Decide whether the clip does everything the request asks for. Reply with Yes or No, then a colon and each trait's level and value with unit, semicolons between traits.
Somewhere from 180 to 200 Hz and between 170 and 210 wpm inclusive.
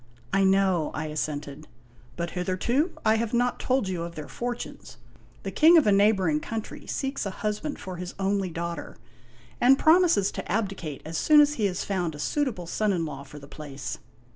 Yes: high, 190 Hz; average, 195 wpm